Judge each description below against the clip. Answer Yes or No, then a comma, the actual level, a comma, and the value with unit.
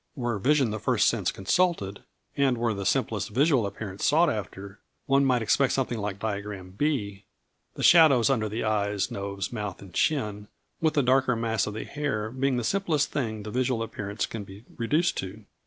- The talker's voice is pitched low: Yes, low, 115 Hz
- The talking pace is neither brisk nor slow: Yes, average, 180 wpm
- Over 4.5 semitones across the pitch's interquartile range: Yes, average, 5.0 semitones